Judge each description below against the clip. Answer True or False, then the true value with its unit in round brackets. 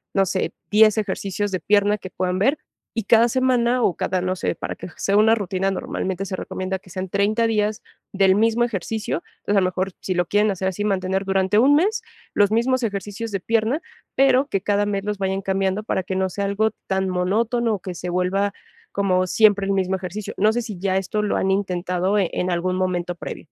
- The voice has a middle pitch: False (195 Hz)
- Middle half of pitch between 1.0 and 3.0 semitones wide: True (2.4 semitones)